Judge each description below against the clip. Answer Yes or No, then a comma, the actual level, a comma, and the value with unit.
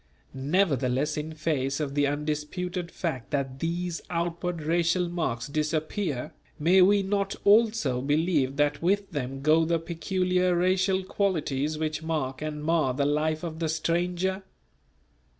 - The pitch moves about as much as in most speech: Yes, average, 3.5 semitones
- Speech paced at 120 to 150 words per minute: Yes, slow, 135 wpm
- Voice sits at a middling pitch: Yes, medium, 160 Hz